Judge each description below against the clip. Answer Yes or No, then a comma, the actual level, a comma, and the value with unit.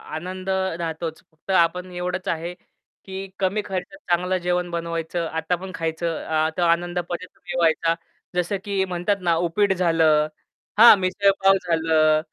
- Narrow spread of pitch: Yes, narrow, 2.2 semitones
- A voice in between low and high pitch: Yes, medium, 175 Hz